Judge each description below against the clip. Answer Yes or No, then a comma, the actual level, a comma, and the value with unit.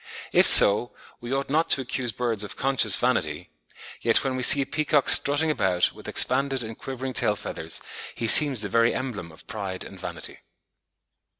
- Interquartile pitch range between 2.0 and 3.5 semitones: No, average, 4.3 semitones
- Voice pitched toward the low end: Yes, low, 125 Hz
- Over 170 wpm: Yes, average, 180 wpm